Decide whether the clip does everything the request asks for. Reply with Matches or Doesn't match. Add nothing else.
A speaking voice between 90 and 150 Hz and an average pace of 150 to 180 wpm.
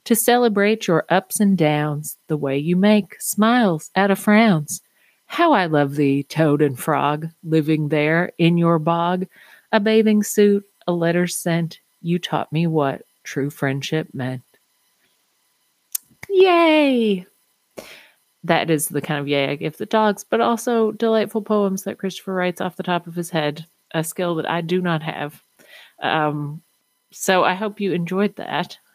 Doesn't match